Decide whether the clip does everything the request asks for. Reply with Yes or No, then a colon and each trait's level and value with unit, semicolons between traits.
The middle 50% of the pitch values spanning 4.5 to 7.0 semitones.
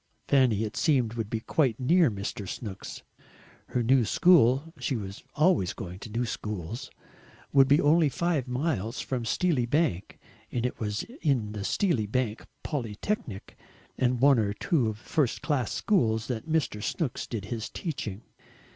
Yes: average, 5.2 semitones